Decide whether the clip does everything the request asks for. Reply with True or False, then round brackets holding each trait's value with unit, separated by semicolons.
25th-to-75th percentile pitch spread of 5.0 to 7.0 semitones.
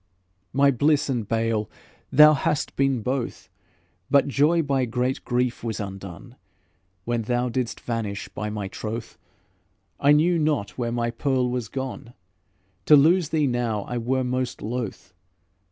False (3.4 semitones)